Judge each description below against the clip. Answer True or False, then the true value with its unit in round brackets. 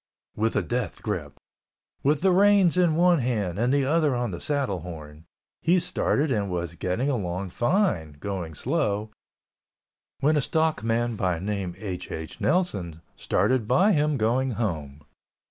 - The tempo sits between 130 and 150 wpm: True (145 wpm)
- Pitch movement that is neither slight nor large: False (8.6 semitones)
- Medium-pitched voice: False (115 Hz)